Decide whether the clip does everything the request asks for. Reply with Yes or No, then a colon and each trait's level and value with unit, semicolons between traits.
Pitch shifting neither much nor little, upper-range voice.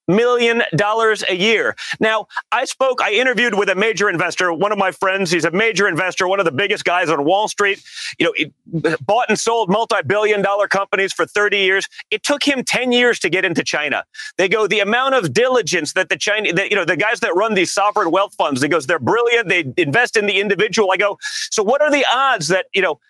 Yes: average, 3.8 semitones; high, 210 Hz